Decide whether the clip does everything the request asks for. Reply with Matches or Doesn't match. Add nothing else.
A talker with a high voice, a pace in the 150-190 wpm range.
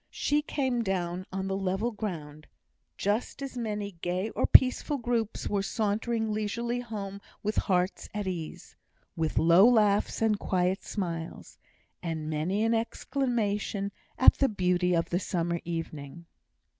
Doesn't match